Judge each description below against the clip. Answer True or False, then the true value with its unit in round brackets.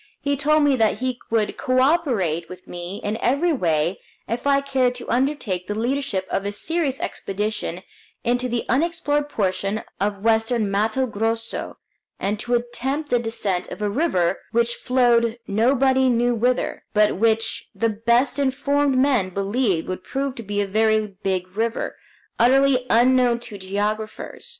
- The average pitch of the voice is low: False (230 Hz)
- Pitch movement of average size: True (4.2 semitones)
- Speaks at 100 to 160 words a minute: True (155 wpm)